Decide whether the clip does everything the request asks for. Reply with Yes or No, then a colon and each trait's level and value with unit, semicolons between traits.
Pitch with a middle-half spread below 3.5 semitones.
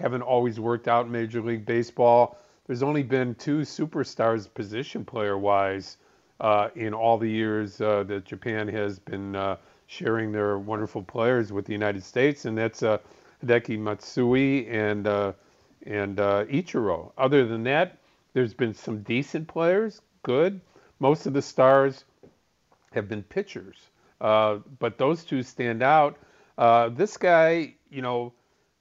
No: average, 4.1 semitones